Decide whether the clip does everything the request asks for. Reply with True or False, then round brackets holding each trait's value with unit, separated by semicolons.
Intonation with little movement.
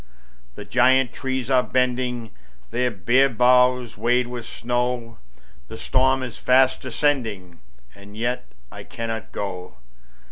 True (2.1 semitones)